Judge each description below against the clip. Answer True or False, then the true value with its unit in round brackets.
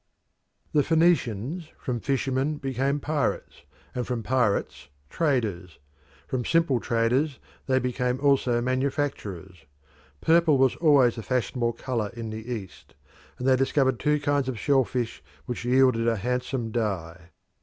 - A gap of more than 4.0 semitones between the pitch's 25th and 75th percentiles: False (3.3 semitones)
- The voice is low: True (125 Hz)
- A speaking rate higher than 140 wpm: False (135 wpm)